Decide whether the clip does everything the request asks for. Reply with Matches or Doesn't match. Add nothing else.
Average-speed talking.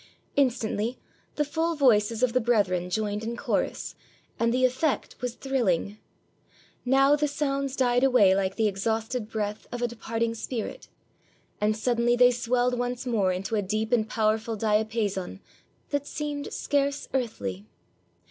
Matches